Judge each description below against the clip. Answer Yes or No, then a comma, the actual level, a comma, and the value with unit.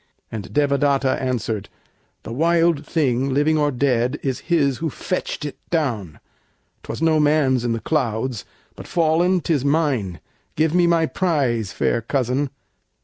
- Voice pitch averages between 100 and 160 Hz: Yes, medium, 140 Hz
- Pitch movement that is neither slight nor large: Yes, average, 4.5 semitones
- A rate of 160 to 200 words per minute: No, average, 145 wpm